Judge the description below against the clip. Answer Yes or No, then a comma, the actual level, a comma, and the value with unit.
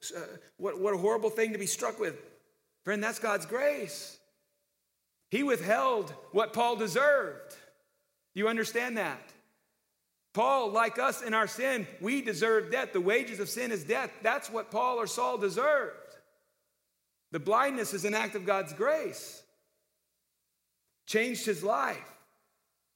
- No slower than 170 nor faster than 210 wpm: No, average, 145 wpm